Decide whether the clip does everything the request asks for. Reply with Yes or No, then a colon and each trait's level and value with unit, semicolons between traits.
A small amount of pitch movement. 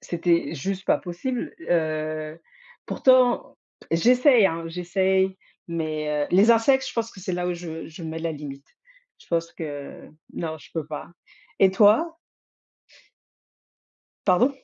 No: average, 4.4 semitones